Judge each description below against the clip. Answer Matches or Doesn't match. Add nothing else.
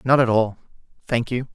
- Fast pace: Doesn't match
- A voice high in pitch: Doesn't match